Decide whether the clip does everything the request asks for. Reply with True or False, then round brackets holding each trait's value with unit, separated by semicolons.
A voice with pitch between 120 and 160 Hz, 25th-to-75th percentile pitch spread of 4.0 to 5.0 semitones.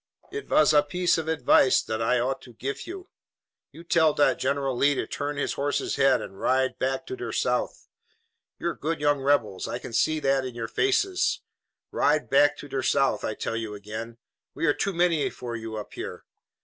True (140 Hz; 4.4 semitones)